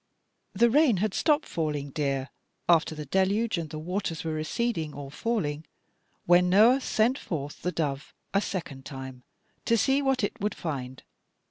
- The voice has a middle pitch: Yes, medium, 170 Hz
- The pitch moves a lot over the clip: Yes, wide, 6.8 semitones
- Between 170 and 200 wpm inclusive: No, average, 160 wpm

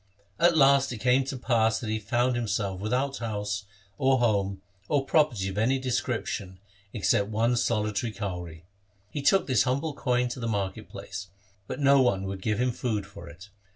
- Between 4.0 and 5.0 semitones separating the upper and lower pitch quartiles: Yes, average, 4.4 semitones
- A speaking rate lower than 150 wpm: No, average, 180 wpm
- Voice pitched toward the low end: Yes, low, 115 Hz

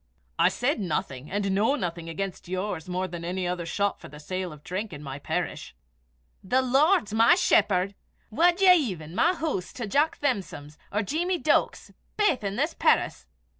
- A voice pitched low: No, high, 195 Hz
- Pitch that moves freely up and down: Yes, wide, 7.6 semitones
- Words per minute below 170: No, average, 180 wpm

